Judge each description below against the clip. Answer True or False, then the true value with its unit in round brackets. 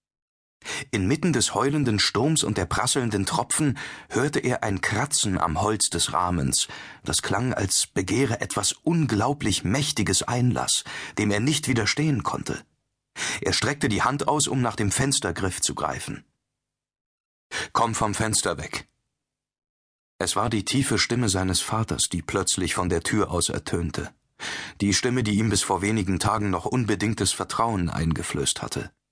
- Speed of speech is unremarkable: True (145 wpm)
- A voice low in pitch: True (105 Hz)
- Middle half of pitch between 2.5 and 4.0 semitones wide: False (4.6 semitones)